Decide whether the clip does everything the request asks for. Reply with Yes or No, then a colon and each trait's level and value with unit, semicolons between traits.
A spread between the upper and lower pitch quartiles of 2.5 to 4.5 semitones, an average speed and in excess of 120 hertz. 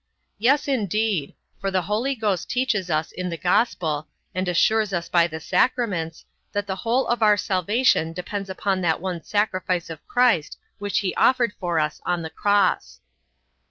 Yes: average, 4.1 semitones; average, 165 wpm; high, 190 Hz